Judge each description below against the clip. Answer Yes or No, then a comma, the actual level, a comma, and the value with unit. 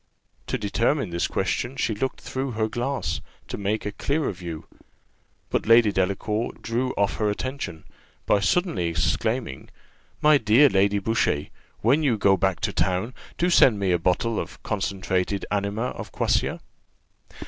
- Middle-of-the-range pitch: No, low, 105 Hz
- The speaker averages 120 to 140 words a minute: No, average, 150 wpm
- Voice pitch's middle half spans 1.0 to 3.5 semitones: No, average, 4.6 semitones